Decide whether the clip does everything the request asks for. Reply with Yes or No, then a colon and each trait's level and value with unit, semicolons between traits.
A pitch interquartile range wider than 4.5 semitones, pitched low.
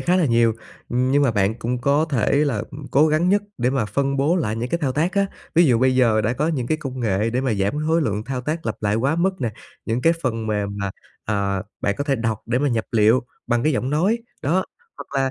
Yes: average, 5.0 semitones; low, 130 Hz